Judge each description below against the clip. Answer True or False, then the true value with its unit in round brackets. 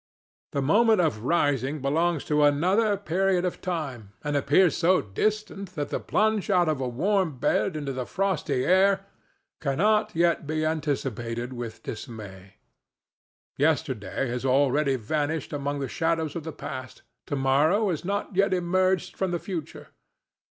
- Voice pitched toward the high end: False (155 Hz)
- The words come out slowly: False (150 wpm)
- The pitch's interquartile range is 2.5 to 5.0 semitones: False (5.5 semitones)